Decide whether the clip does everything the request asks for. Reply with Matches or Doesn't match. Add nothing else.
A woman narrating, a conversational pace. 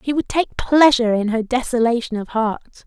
Matches